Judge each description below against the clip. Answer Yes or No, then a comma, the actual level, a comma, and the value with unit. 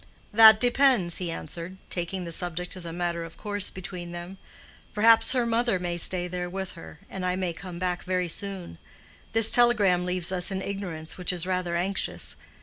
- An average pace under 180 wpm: No, average, 185 wpm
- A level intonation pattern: Yes, narrow, 2.3 semitones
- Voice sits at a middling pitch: Yes, medium, 180 Hz